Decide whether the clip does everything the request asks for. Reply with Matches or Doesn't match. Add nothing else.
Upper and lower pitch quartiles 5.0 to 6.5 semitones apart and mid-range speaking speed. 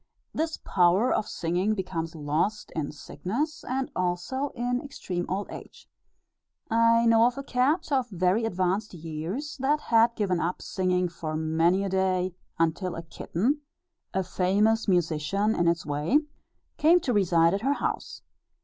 Matches